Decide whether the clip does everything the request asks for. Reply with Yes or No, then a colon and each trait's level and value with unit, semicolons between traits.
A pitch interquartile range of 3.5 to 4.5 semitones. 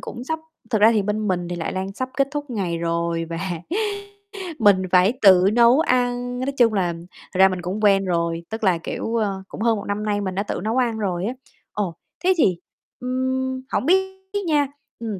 No: average, 5.0 semitones